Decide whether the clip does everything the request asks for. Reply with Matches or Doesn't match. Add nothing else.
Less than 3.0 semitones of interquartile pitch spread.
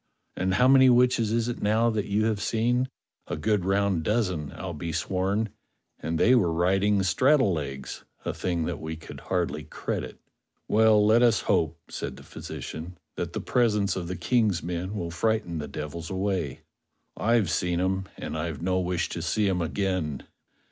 Doesn't match